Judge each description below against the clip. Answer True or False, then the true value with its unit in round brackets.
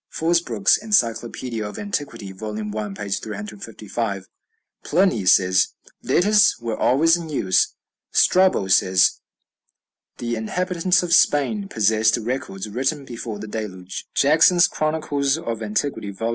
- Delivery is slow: True (115 wpm)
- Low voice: True (115 Hz)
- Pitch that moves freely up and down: True (7.2 semitones)